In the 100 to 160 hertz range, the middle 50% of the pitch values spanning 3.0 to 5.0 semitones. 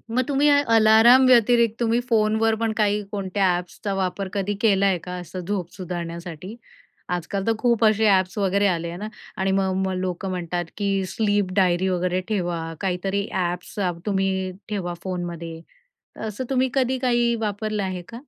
No: high, 195 Hz; average, 3.4 semitones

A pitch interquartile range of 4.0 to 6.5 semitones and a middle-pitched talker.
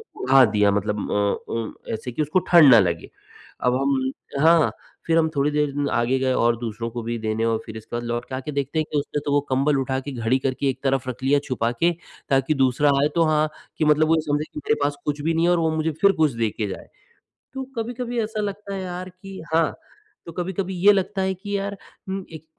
Yes: average, 5.2 semitones; medium, 145 Hz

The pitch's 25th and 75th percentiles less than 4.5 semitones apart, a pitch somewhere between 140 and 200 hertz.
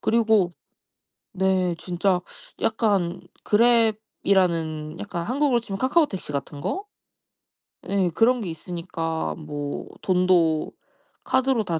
No: average, 5.0 semitones; high, 190 Hz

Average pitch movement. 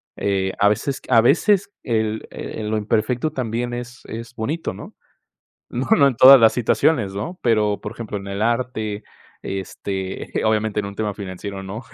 Yes: average, 3.3 semitones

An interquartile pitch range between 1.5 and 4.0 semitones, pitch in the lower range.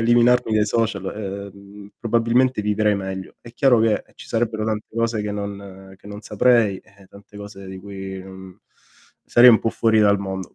Yes: narrow, 2.6 semitones; low, 105 Hz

